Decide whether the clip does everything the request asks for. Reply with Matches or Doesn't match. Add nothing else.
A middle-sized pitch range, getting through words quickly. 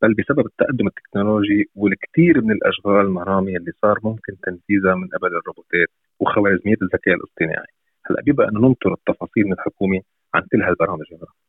Doesn't match